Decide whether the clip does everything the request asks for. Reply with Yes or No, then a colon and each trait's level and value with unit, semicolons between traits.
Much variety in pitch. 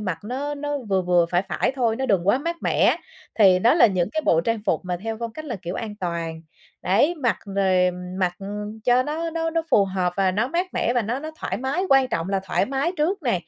Yes: wide, 7.3 semitones